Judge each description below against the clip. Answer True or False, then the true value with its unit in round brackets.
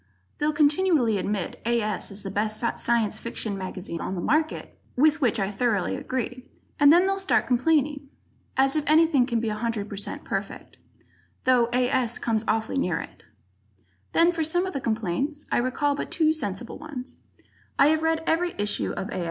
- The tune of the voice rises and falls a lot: True (5.9 semitones)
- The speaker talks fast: False (175 wpm)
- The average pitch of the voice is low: False (255 Hz)